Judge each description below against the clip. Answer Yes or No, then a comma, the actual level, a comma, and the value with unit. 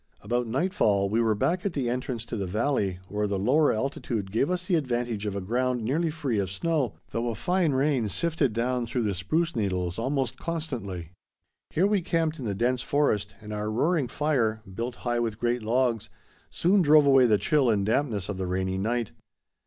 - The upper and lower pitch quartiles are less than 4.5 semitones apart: No, wide, 5.6 semitones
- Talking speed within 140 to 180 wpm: No, average, 200 wpm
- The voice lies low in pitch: Yes, low, 120 Hz